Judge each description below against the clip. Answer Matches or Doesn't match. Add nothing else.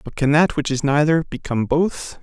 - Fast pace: Matches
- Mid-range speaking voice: Matches